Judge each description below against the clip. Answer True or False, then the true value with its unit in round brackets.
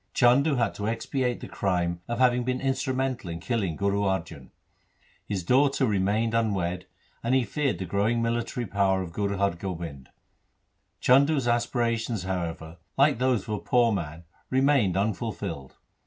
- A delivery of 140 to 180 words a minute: True (155 wpm)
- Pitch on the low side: True (110 Hz)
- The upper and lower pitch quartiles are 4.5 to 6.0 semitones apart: True (5.1 semitones)